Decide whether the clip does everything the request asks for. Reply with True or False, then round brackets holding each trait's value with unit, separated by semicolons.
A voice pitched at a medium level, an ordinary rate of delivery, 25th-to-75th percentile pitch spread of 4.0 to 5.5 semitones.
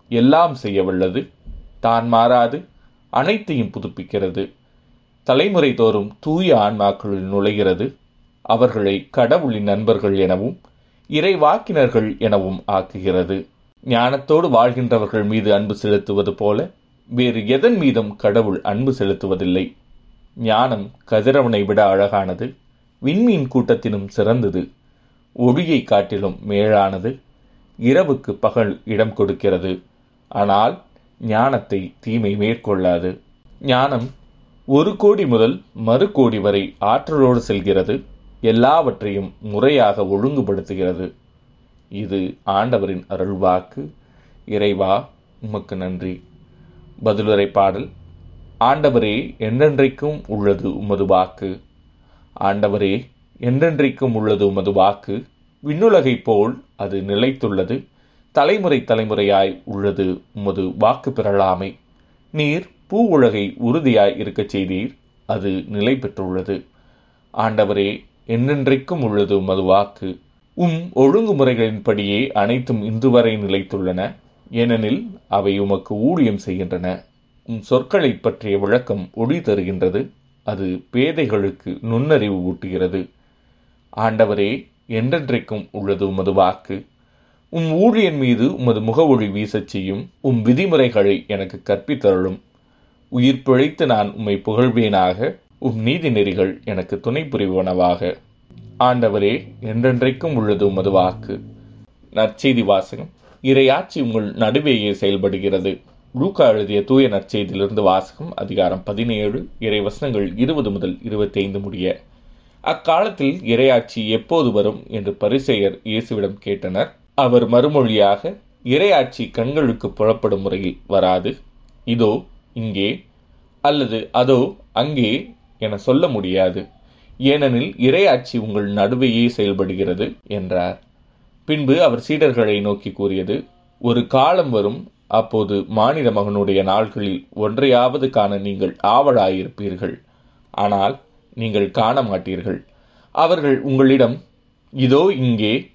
False (105 Hz; 90 wpm; 4.3 semitones)